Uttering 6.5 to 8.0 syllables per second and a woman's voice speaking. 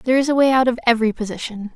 Yes: 7.9 syllables/s; female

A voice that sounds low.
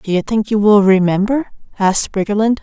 No: high, 210 Hz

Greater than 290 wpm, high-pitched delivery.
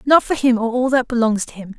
Yes: fast, 305 wpm; high, 240 Hz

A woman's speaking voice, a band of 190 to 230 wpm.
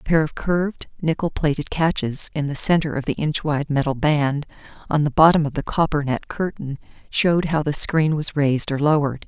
Yes: female; average, 200 wpm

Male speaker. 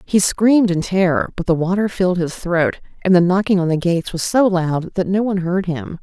No: female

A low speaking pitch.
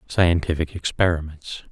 Yes: very low, 80 Hz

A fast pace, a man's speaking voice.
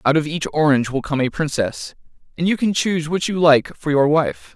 Yes: fast, 235 wpm; male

